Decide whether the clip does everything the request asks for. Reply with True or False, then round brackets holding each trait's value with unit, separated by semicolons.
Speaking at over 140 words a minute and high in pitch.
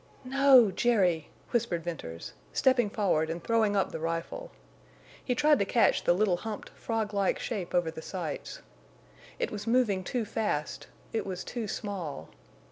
True (150 wpm; 205 Hz)